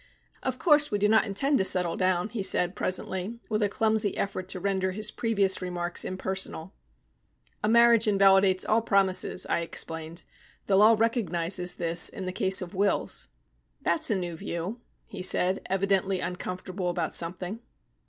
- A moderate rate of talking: Yes, average, 160 wpm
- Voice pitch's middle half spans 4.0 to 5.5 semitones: No, average, 2.8 semitones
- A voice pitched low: No, high, 190 Hz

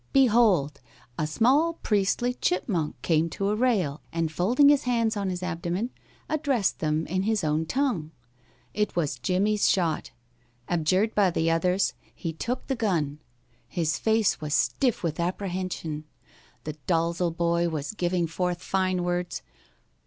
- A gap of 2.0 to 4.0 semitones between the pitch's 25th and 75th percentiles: No, average, 4.7 semitones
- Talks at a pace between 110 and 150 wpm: Yes, average, 145 wpm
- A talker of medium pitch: Yes, medium, 180 Hz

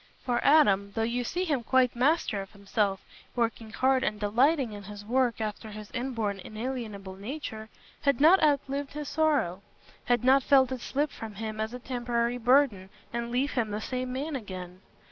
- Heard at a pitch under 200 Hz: No, high, 240 Hz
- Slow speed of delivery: No, average, 175 wpm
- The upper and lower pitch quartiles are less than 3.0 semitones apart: No, average, 4.0 semitones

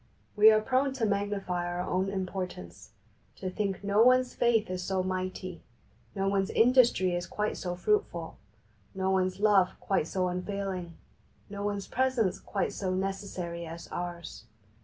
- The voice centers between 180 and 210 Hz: Yes, high, 190 Hz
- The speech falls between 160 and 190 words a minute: No, average, 150 wpm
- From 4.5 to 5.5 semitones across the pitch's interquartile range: No, narrow, 2.4 semitones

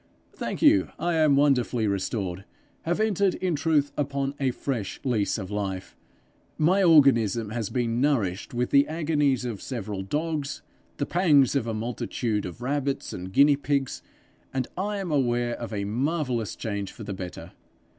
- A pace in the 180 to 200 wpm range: No, average, 165 wpm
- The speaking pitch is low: Yes, low, 130 Hz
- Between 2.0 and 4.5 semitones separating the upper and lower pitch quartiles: No, average, 5.2 semitones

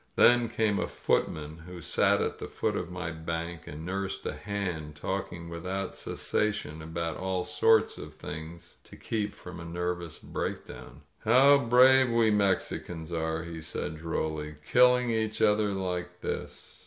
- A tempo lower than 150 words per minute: No, average, 160 wpm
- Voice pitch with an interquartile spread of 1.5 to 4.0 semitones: No, average, 4.4 semitones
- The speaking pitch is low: Yes, very low, 90 Hz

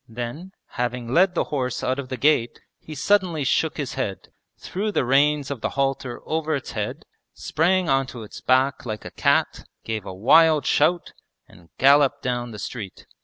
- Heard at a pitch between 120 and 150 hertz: Yes, low, 135 Hz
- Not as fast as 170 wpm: No, average, 175 wpm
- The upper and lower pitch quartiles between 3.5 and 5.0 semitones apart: Yes, average, 4.2 semitones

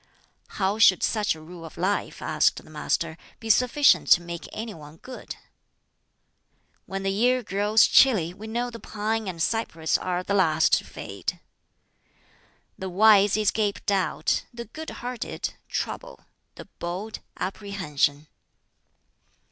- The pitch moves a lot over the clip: No, average, 4.4 semitones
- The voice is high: Yes, high, 200 Hz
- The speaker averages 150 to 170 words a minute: No, slow, 135 wpm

